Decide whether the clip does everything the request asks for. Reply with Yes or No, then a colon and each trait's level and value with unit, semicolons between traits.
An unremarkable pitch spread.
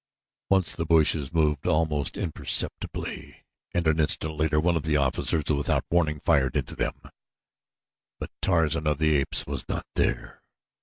No: narrow, 1.8 semitones